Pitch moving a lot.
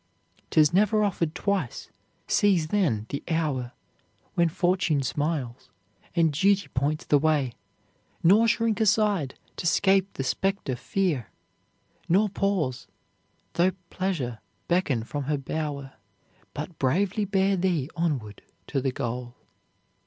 Yes: wide, 6.1 semitones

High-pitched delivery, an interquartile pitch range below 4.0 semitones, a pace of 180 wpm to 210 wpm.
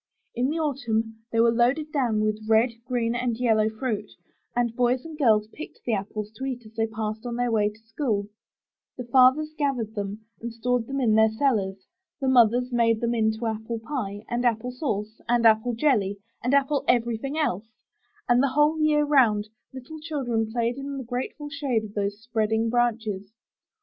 Yes: high, 235 Hz; average, 3.0 semitones; average, 185 wpm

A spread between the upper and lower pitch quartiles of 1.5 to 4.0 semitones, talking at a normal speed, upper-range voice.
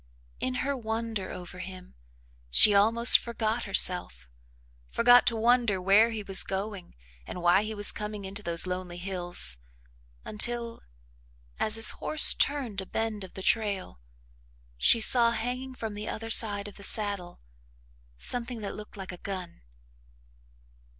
Yes: average, 3.4 semitones; average, 145 wpm; high, 210 Hz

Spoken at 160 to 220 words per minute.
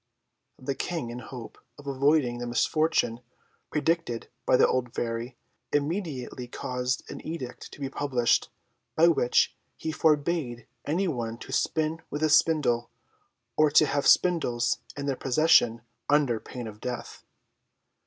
No: average, 140 wpm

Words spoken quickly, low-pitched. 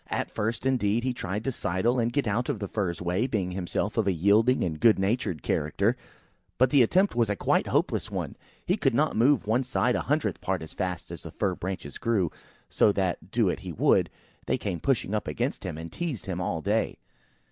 Yes: fast, 220 wpm; low, 105 Hz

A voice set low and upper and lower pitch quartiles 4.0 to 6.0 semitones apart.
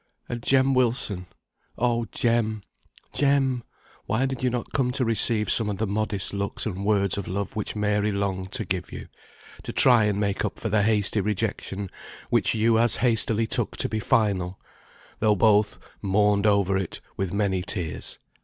No: low, 105 Hz; narrow, 2.6 semitones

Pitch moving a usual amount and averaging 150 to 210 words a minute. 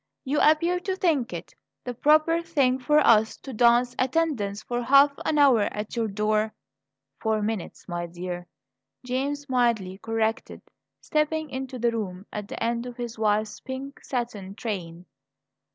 Yes: average, 4.8 semitones; average, 155 wpm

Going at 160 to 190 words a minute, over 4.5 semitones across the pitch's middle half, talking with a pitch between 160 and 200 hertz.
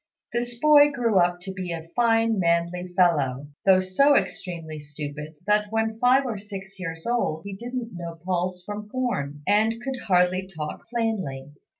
Yes: average, 165 wpm; average, 5.2 semitones; high, 190 Hz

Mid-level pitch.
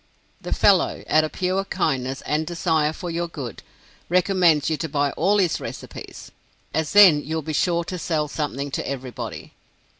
Yes: medium, 160 Hz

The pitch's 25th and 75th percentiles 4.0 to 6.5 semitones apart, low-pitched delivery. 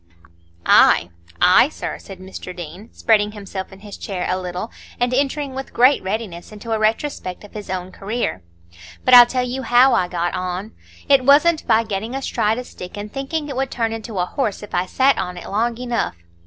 No: average, 5.1 semitones; high, 220 Hz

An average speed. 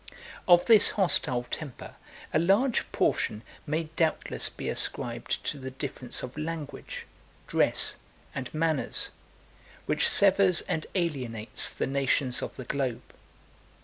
No: slow, 120 wpm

